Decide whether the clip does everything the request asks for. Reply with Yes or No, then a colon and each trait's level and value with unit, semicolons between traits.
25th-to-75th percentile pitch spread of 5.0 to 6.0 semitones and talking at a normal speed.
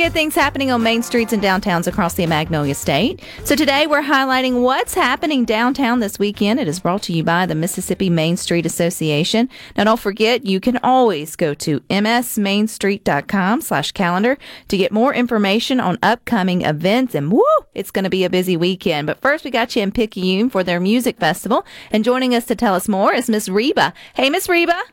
Yes: wide, 5.4 semitones; average, 195 wpm